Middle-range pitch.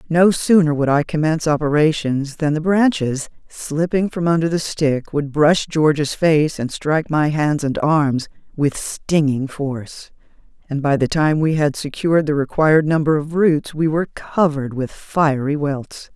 Yes: medium, 150 Hz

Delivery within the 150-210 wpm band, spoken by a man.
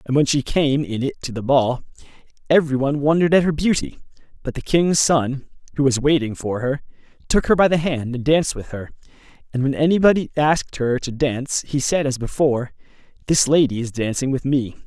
Yes: average, 200 wpm; male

